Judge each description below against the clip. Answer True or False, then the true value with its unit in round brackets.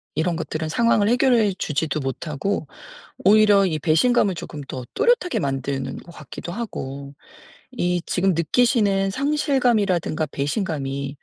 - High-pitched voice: False (180 Hz)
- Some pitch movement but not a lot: False (6.8 semitones)